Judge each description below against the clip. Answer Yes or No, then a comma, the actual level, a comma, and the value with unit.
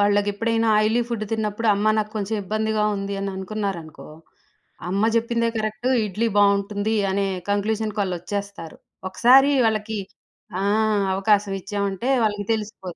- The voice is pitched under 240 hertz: Yes, high, 210 Hz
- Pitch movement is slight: Yes, narrow, 1.7 semitones